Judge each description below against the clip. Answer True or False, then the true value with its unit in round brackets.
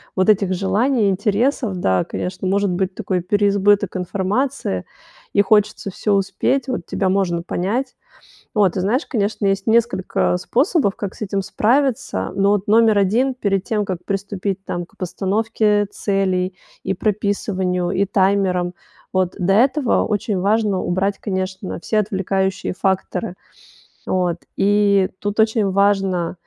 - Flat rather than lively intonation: True (2.1 semitones)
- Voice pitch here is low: False (195 Hz)